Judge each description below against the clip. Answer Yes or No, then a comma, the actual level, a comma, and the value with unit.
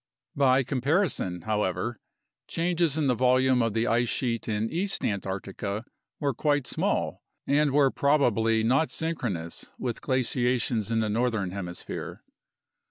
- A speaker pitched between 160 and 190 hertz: No, low, 120 Hz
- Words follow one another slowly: Yes, slow, 130 wpm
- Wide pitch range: No, average, 4.5 semitones